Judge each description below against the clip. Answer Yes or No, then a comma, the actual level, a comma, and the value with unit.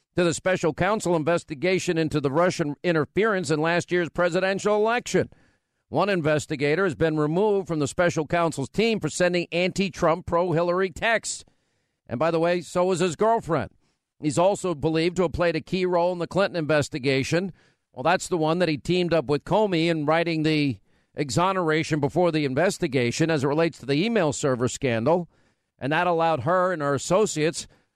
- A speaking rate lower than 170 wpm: No, average, 180 wpm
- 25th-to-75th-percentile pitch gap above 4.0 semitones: No, average, 2.7 semitones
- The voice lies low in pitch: No, medium, 170 Hz